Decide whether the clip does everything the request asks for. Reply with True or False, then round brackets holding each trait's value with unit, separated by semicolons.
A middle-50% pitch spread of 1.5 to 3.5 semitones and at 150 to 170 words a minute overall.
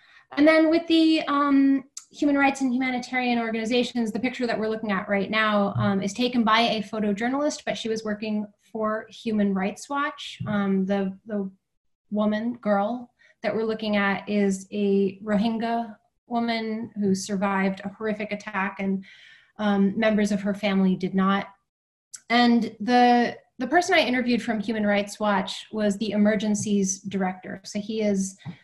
True (3.0 semitones; 155 wpm)